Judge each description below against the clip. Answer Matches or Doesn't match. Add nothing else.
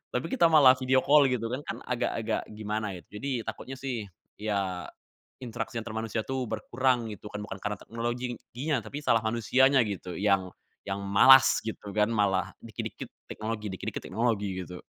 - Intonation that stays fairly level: Doesn't match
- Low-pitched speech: Matches